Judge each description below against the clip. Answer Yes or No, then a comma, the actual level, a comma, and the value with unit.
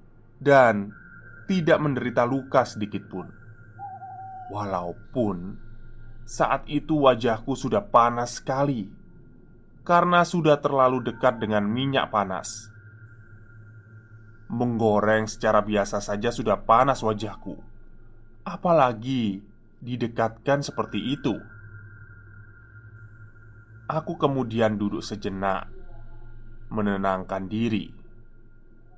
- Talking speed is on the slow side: Yes, slow, 75 wpm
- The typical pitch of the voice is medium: No, low, 115 Hz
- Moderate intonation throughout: Yes, average, 3.0 semitones